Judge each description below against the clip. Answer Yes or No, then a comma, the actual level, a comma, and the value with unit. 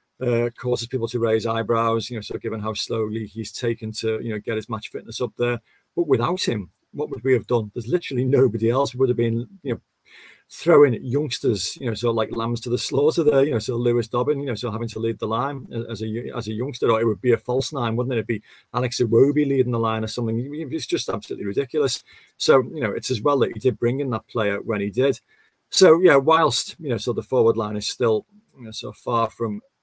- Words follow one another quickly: Yes, fast, 270 wpm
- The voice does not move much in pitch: Yes, narrow, 2.3 semitones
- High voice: No, low, 120 Hz